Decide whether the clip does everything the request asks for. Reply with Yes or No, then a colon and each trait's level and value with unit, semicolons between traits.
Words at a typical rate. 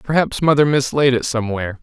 Yes: average, 165 wpm